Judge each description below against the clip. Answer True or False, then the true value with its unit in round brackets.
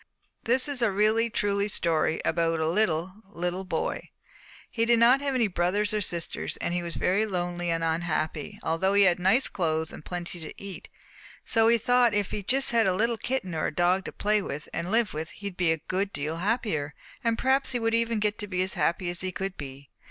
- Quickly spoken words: True (225 wpm)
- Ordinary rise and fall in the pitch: True (4.7 semitones)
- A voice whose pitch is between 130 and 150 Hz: False (190 Hz)